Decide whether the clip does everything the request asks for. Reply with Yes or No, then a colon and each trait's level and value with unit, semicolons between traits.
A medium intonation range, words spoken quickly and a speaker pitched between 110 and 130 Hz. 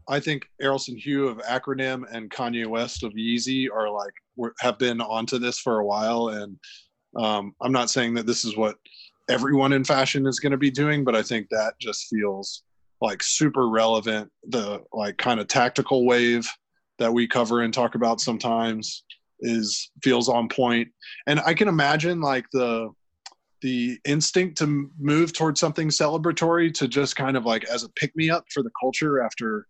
No: average, 3.5 semitones; average, 180 wpm; low, 125 Hz